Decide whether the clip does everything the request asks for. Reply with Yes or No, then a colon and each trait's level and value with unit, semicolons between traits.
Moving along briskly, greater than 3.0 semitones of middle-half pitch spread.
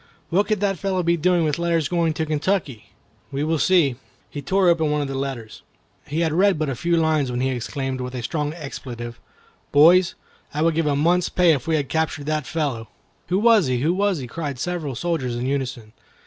Yes: fast, 220 wpm; average, 4.2 semitones